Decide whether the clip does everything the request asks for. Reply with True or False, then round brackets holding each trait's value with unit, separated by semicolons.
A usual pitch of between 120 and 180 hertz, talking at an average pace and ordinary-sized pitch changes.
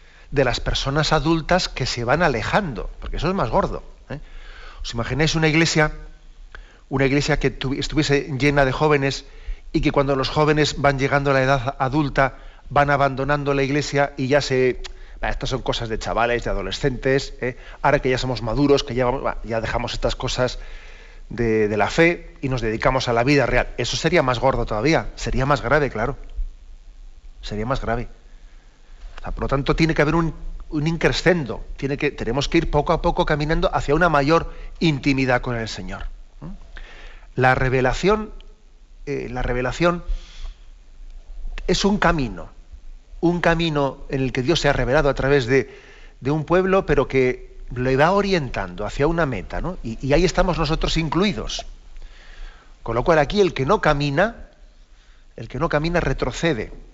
True (140 Hz; 175 wpm; 4.3 semitones)